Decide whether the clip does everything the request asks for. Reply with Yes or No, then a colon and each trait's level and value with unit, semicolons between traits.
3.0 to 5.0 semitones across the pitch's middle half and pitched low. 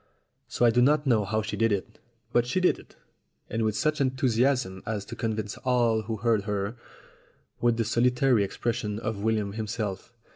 No: narrow, 2.6 semitones; low, 115 Hz